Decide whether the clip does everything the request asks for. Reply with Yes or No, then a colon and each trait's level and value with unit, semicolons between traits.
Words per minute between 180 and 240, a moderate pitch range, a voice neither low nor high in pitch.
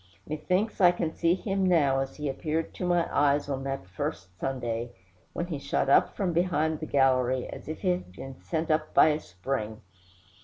Yes: average, 195 wpm; average, 4.4 semitones; medium, 150 Hz